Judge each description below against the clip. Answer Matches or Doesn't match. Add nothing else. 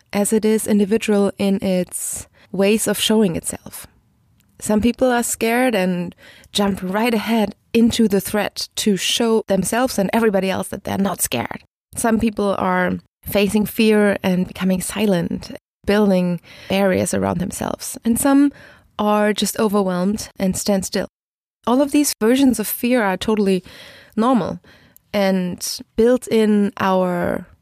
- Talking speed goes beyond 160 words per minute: Doesn't match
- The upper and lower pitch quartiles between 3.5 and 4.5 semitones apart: Doesn't match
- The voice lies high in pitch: Matches